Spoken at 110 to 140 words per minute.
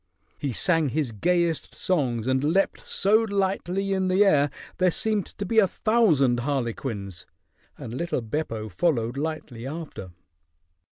Yes: slow, 135 wpm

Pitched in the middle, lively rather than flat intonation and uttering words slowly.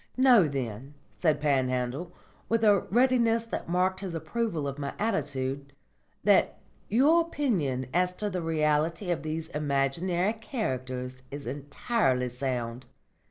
Yes: medium, 155 Hz; wide, 7.4 semitones; slow, 125 wpm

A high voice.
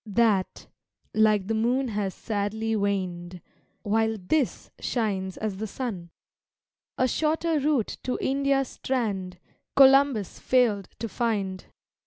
Yes: high, 220 Hz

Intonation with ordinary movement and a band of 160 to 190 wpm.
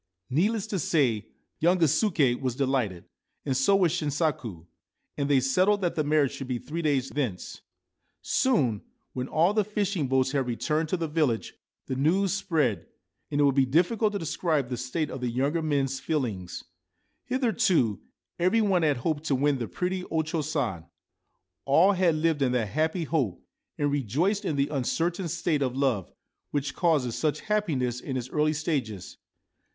Yes: average, 4.7 semitones; average, 175 wpm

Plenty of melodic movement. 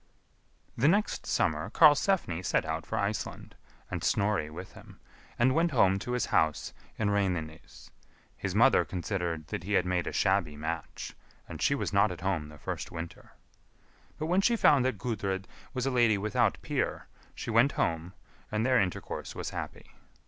Yes: wide, 6.2 semitones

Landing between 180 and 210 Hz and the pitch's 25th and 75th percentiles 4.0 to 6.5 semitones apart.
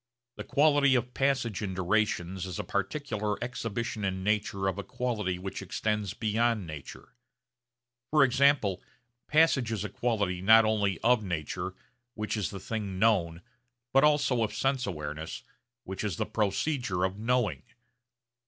No: low, 105 Hz; average, 4.5 semitones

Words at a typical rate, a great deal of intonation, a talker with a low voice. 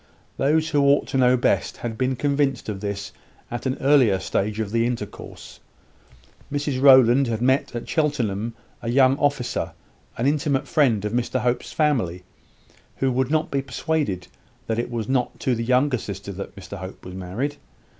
No: average, 175 wpm; average, 4.2 semitones; low, 125 Hz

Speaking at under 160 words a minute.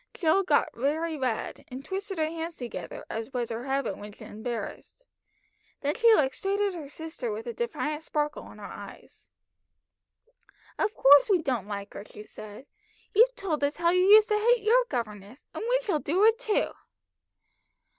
No: average, 175 wpm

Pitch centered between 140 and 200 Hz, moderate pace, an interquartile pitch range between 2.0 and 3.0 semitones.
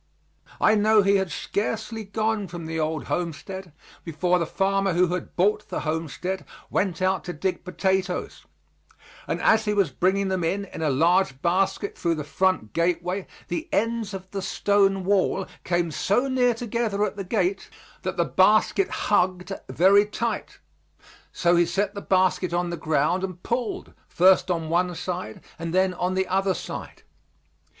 Yes: medium, 185 Hz; average, 165 wpm; narrow, 2.5 semitones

